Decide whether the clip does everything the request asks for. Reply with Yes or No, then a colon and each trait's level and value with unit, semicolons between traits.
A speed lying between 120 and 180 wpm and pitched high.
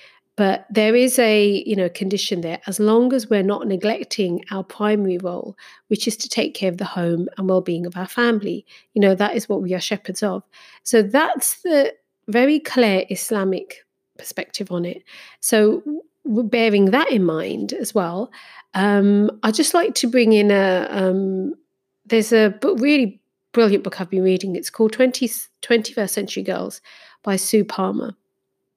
Yes: average, 175 wpm; high, 210 Hz